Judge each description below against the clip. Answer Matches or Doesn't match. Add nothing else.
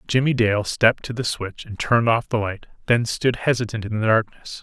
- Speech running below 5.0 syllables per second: Doesn't match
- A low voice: Matches